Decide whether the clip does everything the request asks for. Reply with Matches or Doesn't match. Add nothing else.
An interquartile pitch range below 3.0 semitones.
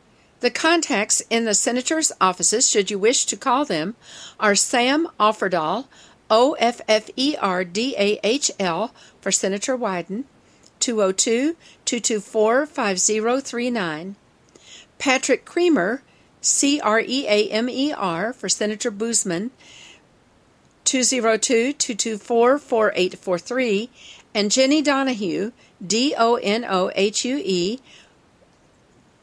Doesn't match